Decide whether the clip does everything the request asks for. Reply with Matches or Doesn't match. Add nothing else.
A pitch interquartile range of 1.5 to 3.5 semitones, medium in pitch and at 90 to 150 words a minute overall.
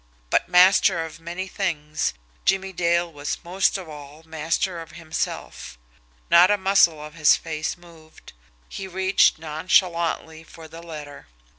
Matches